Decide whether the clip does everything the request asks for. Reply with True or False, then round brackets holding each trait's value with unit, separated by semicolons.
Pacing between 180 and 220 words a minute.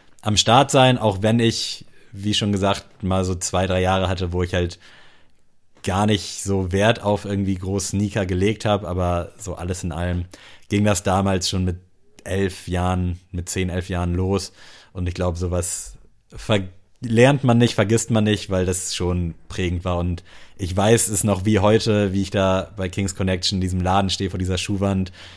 True (190 wpm)